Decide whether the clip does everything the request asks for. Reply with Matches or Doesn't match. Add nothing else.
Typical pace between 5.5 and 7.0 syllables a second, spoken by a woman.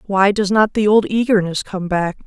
Doesn't match